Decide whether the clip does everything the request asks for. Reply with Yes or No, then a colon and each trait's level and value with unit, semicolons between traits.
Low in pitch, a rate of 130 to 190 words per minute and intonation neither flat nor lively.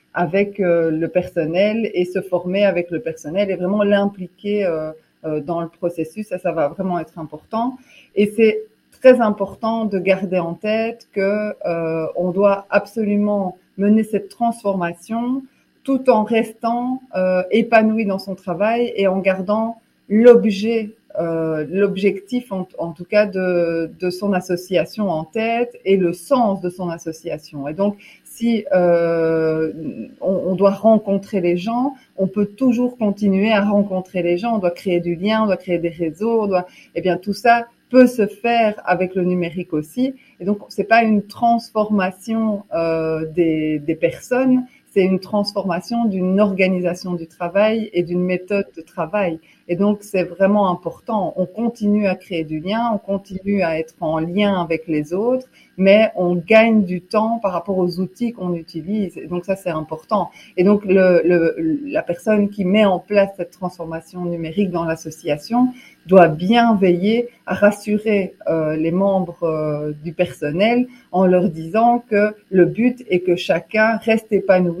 No: high, 195 Hz; average, 165 wpm; average, 3.6 semitones